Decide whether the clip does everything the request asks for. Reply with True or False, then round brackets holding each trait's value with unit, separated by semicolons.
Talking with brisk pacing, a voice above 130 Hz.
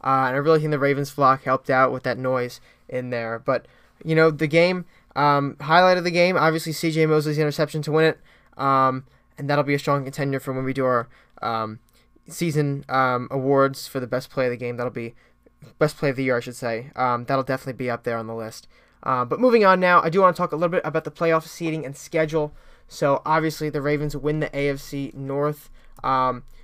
True (230 wpm; 140 Hz)